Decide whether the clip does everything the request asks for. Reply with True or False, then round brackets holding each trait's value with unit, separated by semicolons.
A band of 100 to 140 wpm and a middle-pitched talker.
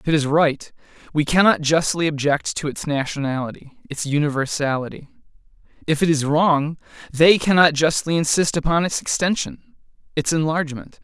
True (135 wpm; 155 Hz)